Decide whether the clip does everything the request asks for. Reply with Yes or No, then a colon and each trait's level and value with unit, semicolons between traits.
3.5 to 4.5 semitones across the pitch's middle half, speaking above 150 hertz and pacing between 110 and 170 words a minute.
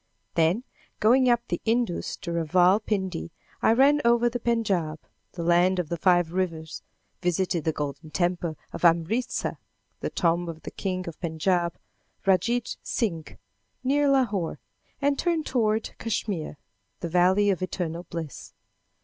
No: average, 5.3 semitones; medium, 185 Hz; average, 140 wpm